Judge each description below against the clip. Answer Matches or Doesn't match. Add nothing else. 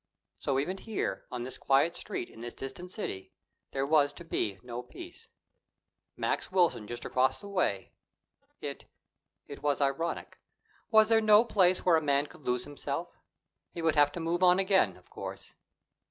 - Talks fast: Doesn't match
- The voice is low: Doesn't match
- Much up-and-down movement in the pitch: Matches